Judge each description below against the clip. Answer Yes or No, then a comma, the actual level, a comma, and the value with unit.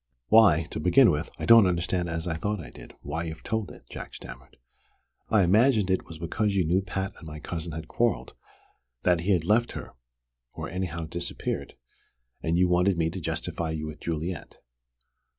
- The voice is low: Yes, very low, 90 Hz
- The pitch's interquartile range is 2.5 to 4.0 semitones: Yes, average, 3.3 semitones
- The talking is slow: No, average, 190 wpm